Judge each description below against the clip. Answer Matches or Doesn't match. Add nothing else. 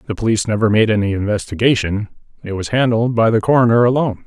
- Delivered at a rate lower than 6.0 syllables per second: Doesn't match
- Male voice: Matches